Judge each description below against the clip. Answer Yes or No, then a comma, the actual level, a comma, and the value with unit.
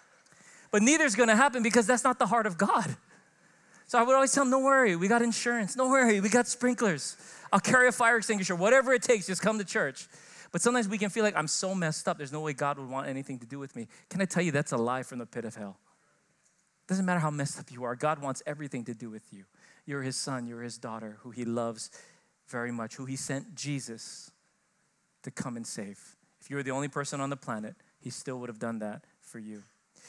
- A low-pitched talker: No, medium, 155 Hz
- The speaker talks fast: Yes, fast, 245 wpm